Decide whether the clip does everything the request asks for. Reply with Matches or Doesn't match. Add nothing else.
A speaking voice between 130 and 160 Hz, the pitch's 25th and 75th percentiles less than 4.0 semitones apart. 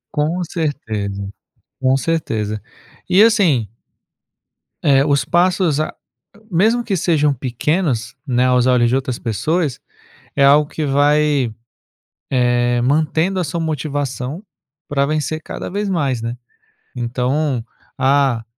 Doesn't match